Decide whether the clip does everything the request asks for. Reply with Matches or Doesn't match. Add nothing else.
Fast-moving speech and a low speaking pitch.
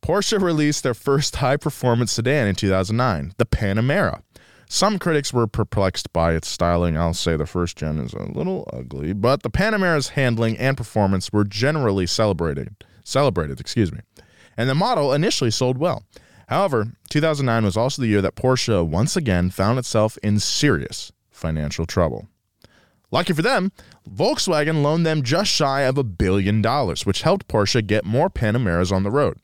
Doesn't match